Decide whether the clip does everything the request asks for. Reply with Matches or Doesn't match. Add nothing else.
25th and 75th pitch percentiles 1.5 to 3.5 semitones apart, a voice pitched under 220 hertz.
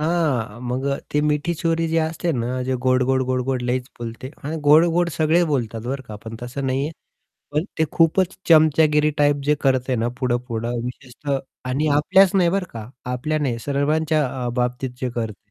Doesn't match